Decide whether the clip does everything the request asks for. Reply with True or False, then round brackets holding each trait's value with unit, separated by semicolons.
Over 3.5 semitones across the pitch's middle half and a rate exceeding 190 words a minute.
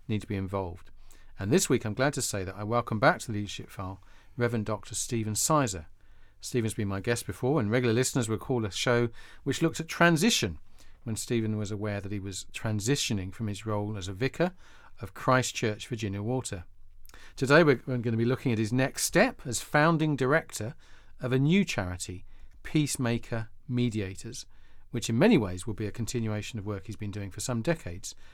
True (4.3 semitones; 200 wpm)